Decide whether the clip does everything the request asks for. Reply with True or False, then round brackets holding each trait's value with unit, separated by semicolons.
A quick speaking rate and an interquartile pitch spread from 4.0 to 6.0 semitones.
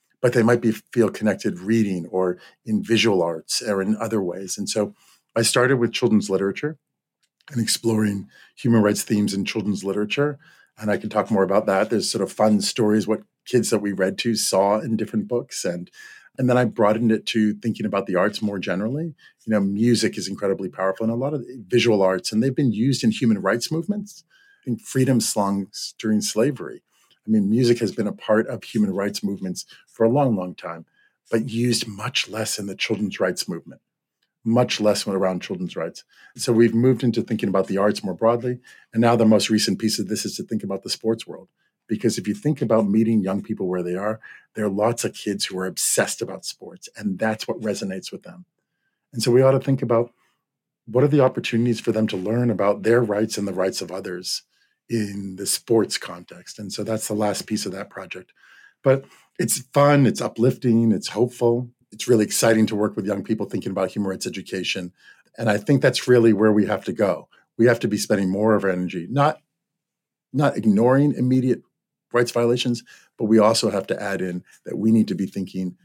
False (210 wpm; 2.9 semitones)